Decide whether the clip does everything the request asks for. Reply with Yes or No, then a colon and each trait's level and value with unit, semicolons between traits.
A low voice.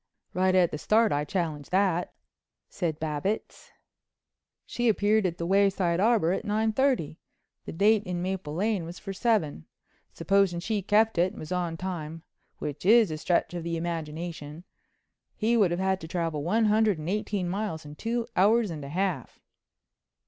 No: medium, 185 Hz